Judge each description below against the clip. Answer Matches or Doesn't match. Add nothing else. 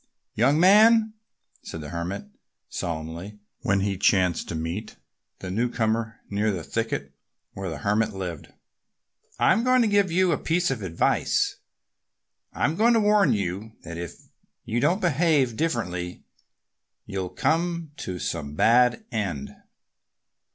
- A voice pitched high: Doesn't match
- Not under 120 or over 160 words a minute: Matches